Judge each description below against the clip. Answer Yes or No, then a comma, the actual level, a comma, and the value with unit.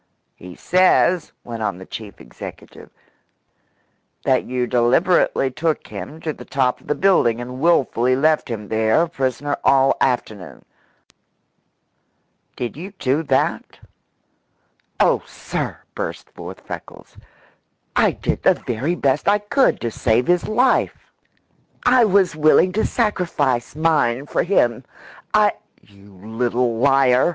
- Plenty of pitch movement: Yes, wide, 6.0 semitones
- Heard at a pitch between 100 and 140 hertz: Yes, low, 135 Hz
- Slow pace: Yes, slow, 130 wpm